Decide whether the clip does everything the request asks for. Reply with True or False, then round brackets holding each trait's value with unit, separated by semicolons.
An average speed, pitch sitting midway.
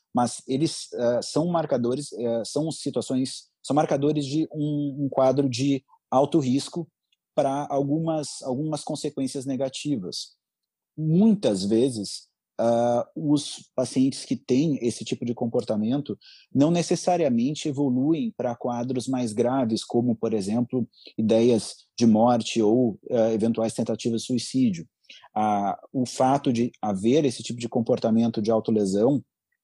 False (130 wpm; 130 Hz)